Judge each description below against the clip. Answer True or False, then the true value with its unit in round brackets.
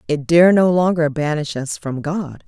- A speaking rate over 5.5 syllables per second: False (4.4 syllables/s)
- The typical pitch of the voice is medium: True (160 Hz)